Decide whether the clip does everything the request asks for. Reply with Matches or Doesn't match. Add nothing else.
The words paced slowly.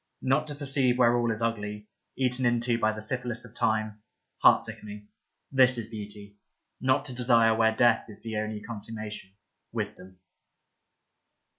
Doesn't match